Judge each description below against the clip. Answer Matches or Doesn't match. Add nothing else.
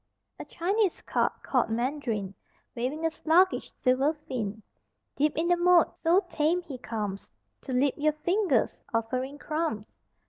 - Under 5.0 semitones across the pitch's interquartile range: Doesn't match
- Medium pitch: Doesn't match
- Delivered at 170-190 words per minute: Doesn't match